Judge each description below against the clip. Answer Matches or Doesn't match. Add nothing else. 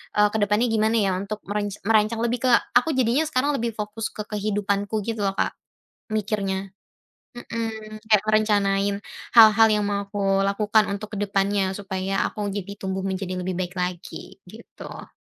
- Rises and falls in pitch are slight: Matches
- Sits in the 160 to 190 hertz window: Doesn't match